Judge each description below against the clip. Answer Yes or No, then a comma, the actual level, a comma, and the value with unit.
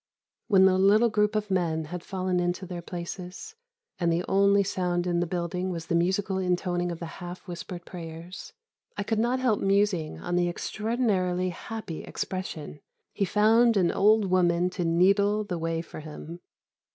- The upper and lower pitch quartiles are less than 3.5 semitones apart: Yes, narrow, 2.6 semitones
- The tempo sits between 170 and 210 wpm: Yes, average, 175 wpm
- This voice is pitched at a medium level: Yes, medium, 180 Hz